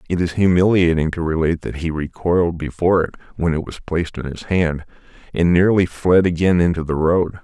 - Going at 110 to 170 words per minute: No, average, 195 wpm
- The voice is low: Yes, very low, 85 Hz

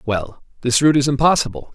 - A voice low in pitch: Yes, low, 125 Hz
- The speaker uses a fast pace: No, average, 170 wpm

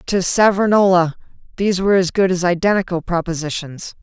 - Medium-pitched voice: Yes, medium, 180 Hz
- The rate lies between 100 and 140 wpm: Yes, slow, 135 wpm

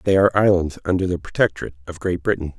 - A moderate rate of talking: No, fast, 210 wpm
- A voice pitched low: Yes, very low, 90 Hz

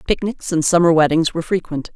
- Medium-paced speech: Yes, average, 185 wpm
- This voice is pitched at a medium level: Yes, medium, 165 Hz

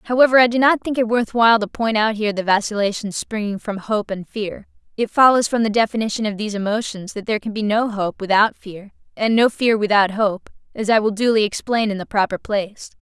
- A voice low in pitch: No, high, 215 Hz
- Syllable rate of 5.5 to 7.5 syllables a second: Yes, 5.8 syllables/s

